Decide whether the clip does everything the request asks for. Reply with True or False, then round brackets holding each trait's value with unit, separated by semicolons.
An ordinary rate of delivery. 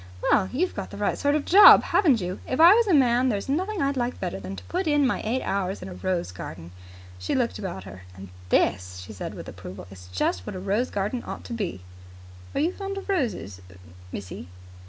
False (230 wpm)